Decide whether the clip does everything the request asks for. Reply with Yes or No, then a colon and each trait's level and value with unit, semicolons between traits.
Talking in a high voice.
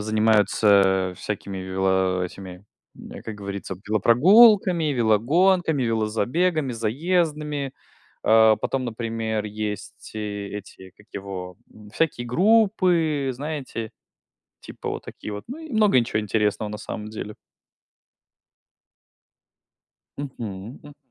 No: low, 110 Hz